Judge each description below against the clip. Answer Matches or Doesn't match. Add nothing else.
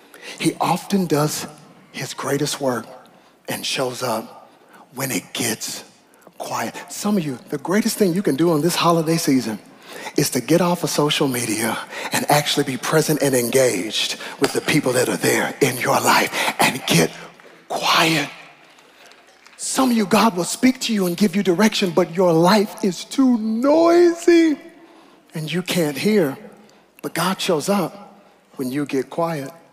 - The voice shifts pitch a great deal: Matches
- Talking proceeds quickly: Doesn't match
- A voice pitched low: Doesn't match